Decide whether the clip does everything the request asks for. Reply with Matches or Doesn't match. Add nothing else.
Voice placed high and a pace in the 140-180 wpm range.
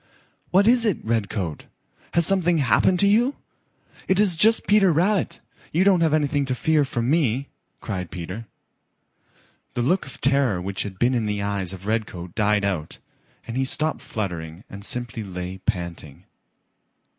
Doesn't match